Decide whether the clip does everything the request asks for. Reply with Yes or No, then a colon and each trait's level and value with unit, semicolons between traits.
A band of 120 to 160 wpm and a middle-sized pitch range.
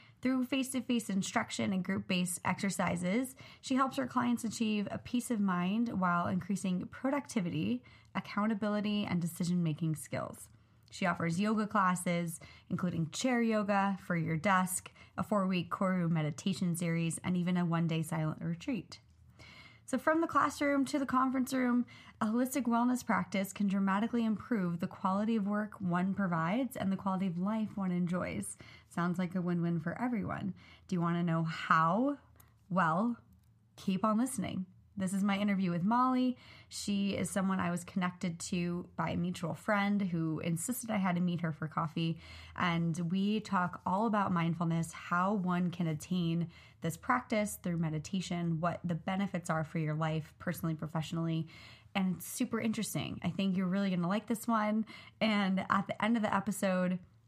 No: average, 170 wpm; average, 4.0 semitones